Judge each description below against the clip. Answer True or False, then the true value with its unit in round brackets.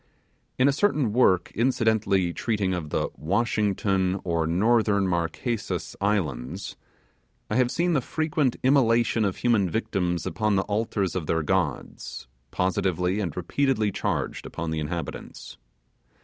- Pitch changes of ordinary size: True (4.9 semitones)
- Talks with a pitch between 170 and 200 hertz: False (100 Hz)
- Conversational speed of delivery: False (130 wpm)